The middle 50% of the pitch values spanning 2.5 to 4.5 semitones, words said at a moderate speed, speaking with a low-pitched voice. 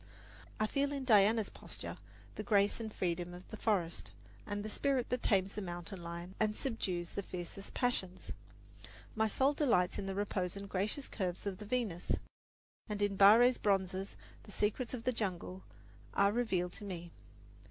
No: average, 3.4 semitones; average, 170 wpm; high, 200 Hz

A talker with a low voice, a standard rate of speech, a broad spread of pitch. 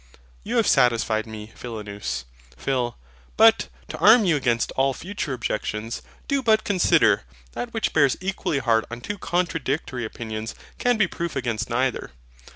Yes: low, 130 Hz; average, 150 wpm; wide, 7.9 semitones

